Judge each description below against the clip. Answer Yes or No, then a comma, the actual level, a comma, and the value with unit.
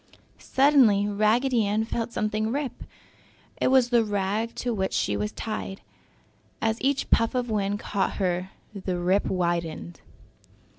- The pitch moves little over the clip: No, average, 3.5 semitones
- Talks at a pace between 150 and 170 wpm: No, average, 140 wpm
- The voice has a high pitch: Yes, high, 215 Hz